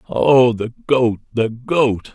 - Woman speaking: No, male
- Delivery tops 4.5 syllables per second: No, 2.9 syllables/s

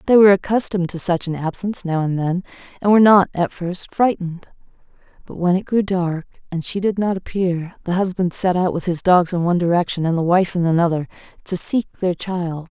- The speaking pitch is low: No, medium, 180 Hz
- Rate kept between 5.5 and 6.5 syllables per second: Yes, 5.7 syllables/s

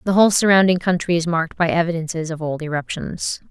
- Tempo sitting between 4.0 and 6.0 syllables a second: No, 6.4 syllables/s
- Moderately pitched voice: Yes, medium, 170 Hz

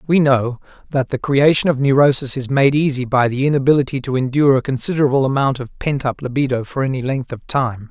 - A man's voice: Yes, male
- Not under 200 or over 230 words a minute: Yes, fast, 205 wpm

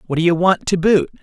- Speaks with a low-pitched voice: No, medium, 175 Hz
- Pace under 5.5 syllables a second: No, 6.3 syllables/s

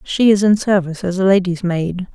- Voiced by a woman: Yes, female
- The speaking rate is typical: No, fast, 225 wpm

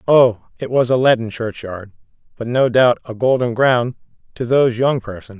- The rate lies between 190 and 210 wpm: No, average, 180 wpm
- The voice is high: No, low, 120 Hz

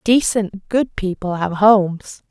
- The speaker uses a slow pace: Yes, slow, 130 wpm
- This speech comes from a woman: Yes, female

